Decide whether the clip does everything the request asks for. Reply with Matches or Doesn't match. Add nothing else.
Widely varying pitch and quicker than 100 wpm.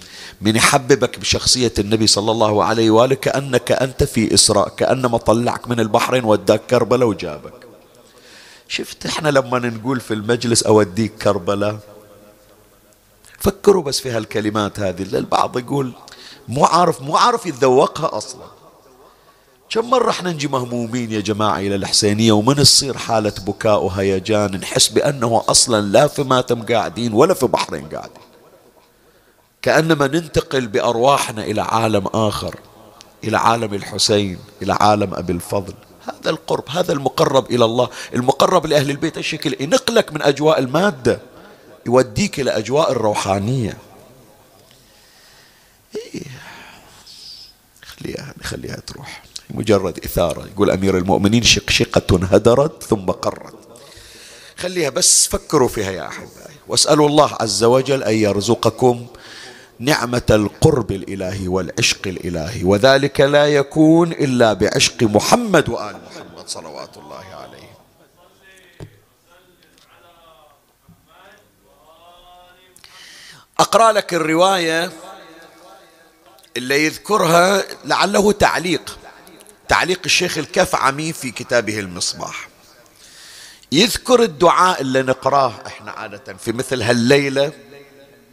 Matches